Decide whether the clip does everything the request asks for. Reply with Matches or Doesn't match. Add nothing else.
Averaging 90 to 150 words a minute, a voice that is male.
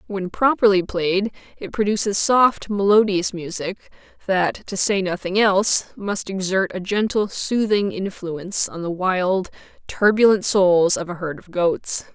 Doesn't match